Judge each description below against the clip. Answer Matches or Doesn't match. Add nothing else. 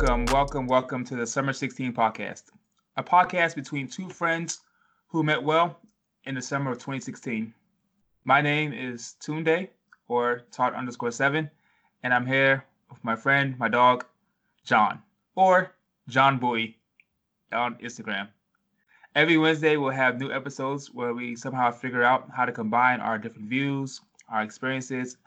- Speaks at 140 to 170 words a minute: Matches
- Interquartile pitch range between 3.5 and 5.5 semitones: Matches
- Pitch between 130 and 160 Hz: Matches